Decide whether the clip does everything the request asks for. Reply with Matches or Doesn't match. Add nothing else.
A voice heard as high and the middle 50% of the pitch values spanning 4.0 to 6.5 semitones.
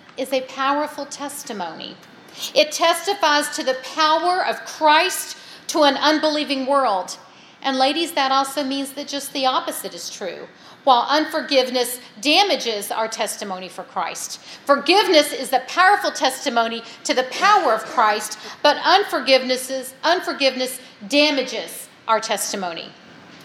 Doesn't match